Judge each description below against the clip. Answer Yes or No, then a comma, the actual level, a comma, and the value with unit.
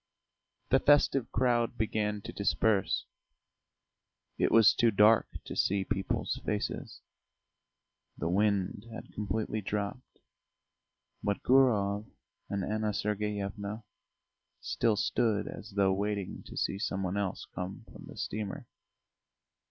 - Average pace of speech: No, slow, 115 wpm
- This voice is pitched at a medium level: No, low, 105 Hz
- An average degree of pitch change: No, narrow, 1.7 semitones